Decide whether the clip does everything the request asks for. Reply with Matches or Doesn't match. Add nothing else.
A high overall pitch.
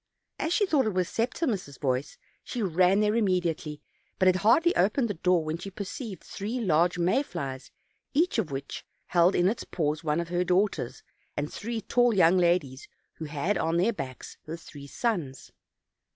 Doesn't match